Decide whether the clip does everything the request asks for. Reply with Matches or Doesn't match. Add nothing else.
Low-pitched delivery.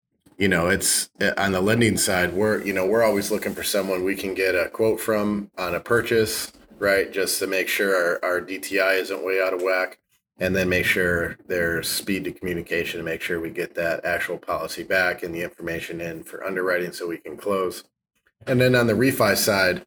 Matches